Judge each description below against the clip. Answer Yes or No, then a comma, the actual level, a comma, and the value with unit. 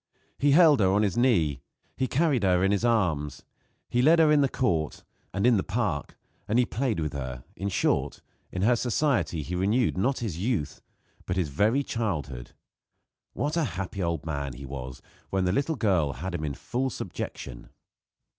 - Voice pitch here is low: Yes, low, 100 Hz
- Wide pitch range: Yes, wide, 8.0 semitones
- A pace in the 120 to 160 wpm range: No, average, 185 wpm